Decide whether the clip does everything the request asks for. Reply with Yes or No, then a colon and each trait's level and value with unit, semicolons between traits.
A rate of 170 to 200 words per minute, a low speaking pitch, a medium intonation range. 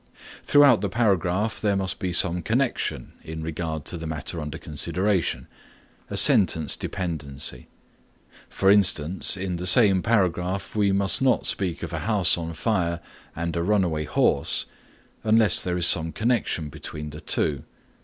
No: average, 150 wpm; very low, 90 Hz; average, 3.9 semitones